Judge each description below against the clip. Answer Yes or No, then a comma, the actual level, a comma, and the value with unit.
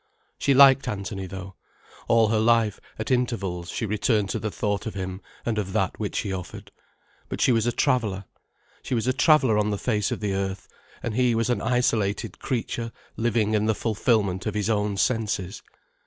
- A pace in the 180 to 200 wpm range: Yes, average, 190 wpm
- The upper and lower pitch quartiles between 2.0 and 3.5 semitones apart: Yes, average, 3.0 semitones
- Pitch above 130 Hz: No, low, 110 Hz